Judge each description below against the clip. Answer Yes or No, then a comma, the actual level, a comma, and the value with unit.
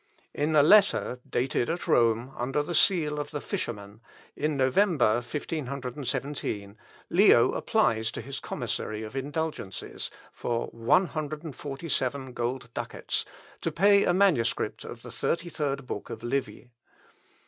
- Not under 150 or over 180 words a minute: No, average, 140 wpm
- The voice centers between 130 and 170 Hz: Yes, low, 135 Hz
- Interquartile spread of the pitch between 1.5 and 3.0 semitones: No, average, 4.3 semitones